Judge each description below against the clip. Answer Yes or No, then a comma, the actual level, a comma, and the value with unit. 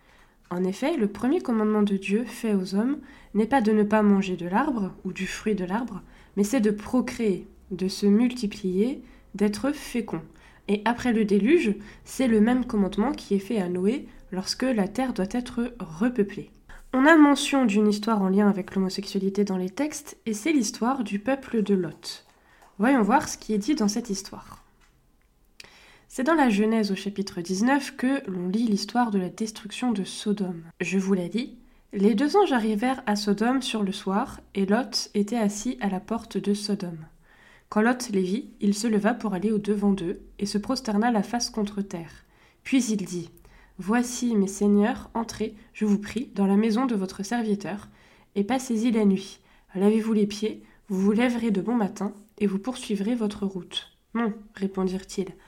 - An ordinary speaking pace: Yes, average, 185 wpm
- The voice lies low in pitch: No, high, 210 Hz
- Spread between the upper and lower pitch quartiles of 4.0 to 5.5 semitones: No, average, 3.5 semitones